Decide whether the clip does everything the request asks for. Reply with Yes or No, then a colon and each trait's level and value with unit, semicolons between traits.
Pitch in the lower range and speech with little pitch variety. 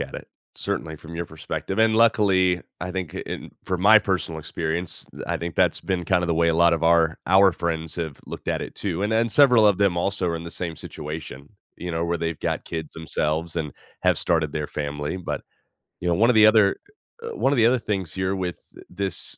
No: very low, 85 Hz; average, 3.2 semitones